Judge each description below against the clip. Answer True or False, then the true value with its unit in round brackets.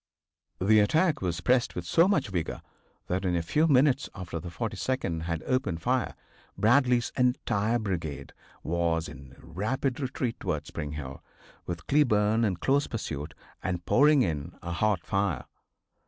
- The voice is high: False (100 Hz)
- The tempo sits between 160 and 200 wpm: False (150 wpm)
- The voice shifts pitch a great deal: True (7.1 semitones)